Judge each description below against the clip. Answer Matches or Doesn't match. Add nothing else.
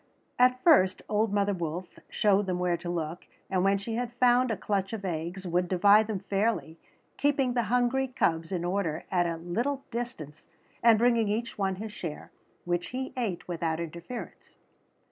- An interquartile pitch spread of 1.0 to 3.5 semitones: Doesn't match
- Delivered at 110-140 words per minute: Doesn't match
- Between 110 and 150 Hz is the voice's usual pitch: Doesn't match